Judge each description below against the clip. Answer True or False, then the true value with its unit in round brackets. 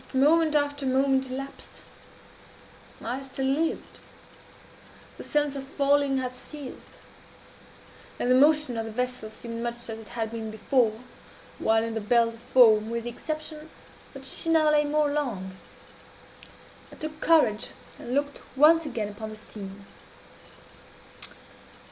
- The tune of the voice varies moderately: True (4.4 semitones)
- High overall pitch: True (260 Hz)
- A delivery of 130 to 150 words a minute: True (140 wpm)